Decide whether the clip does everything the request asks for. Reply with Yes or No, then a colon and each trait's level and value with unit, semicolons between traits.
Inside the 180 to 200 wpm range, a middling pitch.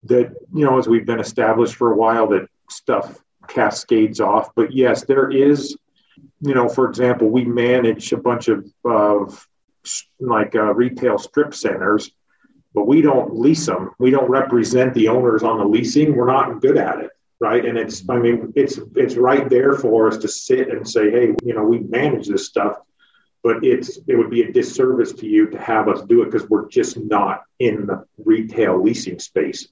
No: average, 195 wpm; low, 130 Hz